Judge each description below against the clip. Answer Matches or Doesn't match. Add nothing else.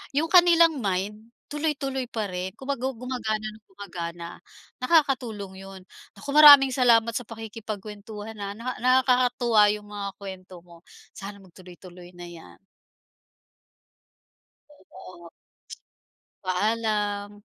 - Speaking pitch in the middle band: Doesn't match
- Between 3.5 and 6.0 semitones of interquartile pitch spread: Matches